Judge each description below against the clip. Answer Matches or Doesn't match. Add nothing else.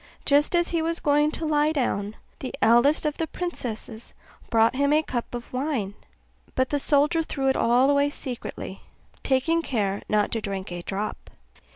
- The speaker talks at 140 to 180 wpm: Matches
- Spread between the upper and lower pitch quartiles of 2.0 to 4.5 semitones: Doesn't match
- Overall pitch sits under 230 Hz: Doesn't match